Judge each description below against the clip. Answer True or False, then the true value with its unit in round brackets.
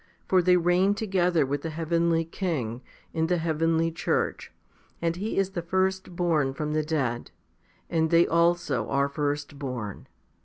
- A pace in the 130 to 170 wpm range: True (145 wpm)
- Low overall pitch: False (165 Hz)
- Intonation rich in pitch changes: False (3.2 semitones)